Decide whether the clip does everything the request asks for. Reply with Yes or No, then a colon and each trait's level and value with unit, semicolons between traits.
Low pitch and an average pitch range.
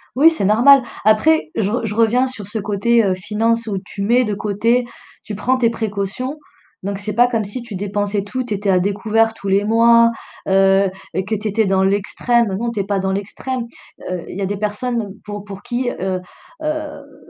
No: high, 210 Hz; average, 3.0 semitones